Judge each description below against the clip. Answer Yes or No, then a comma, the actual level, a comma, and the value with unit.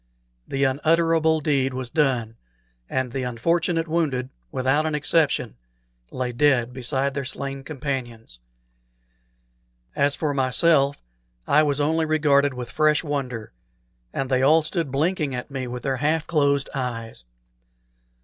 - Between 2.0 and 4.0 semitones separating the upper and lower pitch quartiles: Yes, average, 3.1 semitones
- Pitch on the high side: No, medium, 140 Hz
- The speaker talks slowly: Yes, slow, 130 wpm